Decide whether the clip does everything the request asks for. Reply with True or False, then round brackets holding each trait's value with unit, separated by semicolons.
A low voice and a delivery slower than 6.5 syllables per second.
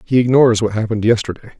False (115 Hz; 8.3 syllables/s)